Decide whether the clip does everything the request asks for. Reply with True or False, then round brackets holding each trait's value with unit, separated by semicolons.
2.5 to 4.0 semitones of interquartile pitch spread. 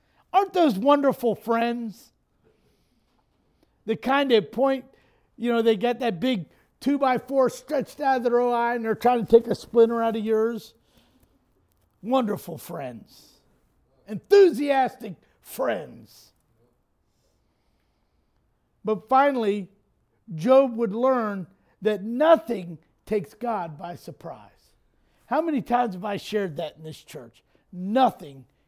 False (4.5 semitones)